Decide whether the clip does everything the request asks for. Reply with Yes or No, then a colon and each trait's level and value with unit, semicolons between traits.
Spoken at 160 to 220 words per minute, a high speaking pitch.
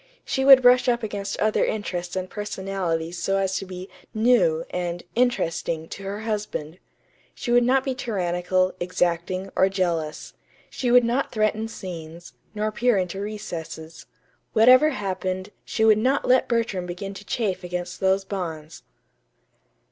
No: average, 150 wpm; high, 195 Hz